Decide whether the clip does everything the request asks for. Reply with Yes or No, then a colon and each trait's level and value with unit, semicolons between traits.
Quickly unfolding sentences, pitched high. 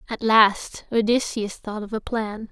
No: average, 165 wpm; high, 220 Hz